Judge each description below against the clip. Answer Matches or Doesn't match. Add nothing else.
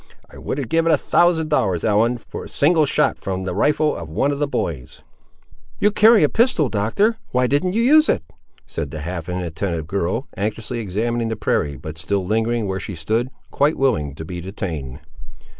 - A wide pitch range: Matches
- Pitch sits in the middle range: Doesn't match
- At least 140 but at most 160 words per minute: Doesn't match